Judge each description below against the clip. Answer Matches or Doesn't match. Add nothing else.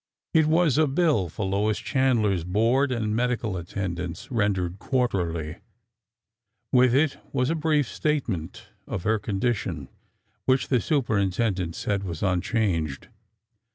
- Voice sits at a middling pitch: Doesn't match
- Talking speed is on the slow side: Matches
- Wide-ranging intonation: Matches